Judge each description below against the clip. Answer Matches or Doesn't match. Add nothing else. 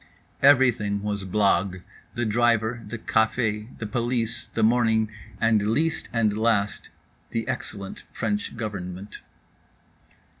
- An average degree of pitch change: Doesn't match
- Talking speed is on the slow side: Matches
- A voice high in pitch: Doesn't match